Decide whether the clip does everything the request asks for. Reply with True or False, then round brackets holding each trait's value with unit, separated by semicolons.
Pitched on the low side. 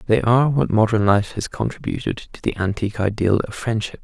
True (110 Hz)